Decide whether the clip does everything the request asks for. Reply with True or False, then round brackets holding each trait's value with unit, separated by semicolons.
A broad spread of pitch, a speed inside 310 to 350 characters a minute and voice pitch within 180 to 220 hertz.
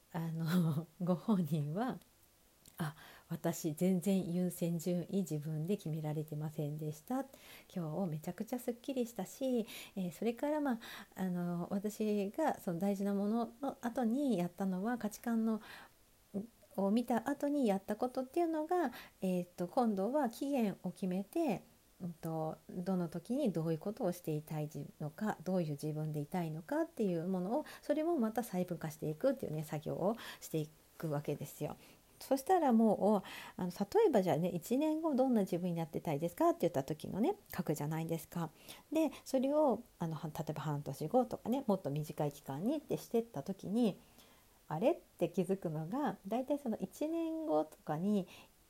True (6.7 semitones; 325 characters per minute; 190 Hz)